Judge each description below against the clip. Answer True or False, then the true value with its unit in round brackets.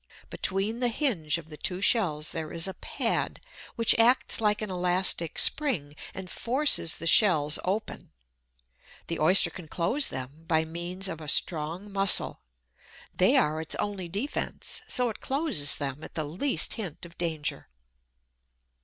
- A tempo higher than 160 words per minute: False (155 wpm)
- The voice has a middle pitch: True (180 Hz)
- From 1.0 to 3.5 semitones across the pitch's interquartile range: False (5.0 semitones)